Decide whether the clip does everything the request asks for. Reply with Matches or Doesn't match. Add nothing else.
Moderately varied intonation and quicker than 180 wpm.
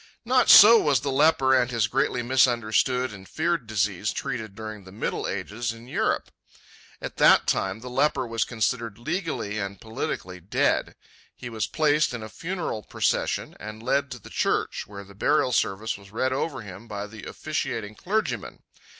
Doesn't match